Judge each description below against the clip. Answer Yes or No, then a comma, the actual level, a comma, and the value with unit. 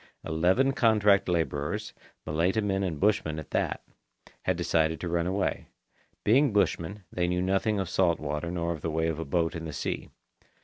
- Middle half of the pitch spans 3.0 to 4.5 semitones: Yes, average, 3.5 semitones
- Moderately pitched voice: No, very low, 85 Hz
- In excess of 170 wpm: Yes, average, 180 wpm